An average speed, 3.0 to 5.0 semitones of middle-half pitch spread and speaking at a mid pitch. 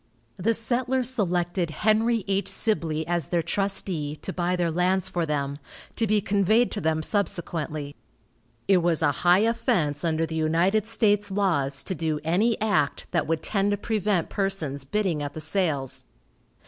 Yes: average, 160 wpm; average, 4.6 semitones; medium, 180 Hz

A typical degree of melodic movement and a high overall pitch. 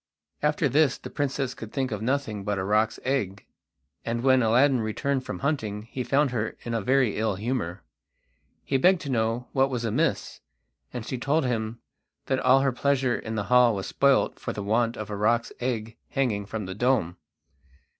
No: average, 3.7 semitones; low, 120 Hz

